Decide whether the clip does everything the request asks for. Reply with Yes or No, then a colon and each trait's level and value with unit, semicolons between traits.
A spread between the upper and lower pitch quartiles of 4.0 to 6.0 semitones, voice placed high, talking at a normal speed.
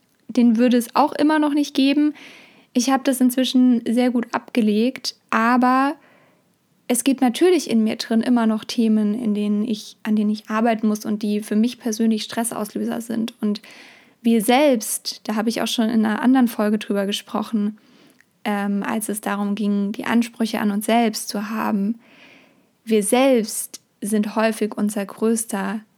No: average, 2.8 semitones; high, 230 Hz; average, 165 wpm